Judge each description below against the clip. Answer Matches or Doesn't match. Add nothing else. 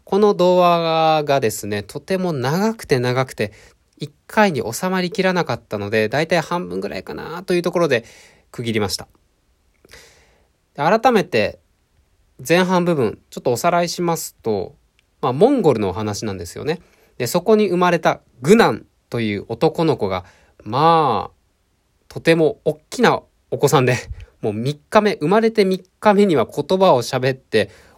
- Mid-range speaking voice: Matches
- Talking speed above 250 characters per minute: Matches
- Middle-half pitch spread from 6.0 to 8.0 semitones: Matches